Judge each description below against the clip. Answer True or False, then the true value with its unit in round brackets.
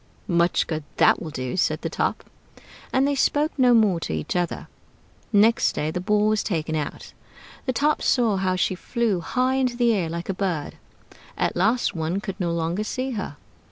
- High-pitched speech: True (195 Hz)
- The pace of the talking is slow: False (195 wpm)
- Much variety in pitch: True (6.0 semitones)